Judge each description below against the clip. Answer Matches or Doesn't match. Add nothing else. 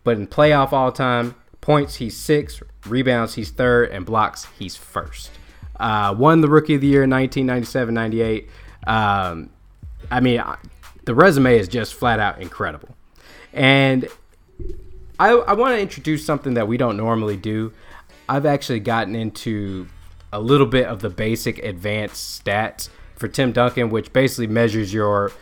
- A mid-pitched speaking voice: Doesn't match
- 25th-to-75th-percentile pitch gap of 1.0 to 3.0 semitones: Doesn't match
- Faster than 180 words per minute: Doesn't match